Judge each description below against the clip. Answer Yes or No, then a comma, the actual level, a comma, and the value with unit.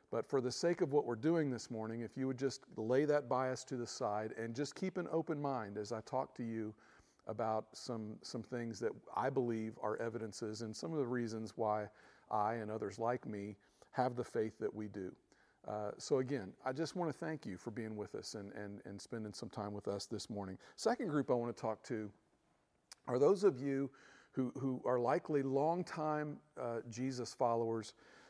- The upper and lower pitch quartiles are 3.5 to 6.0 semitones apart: Yes, average, 3.8 semitones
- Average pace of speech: No, fast, 210 wpm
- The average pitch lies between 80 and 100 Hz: No, low, 120 Hz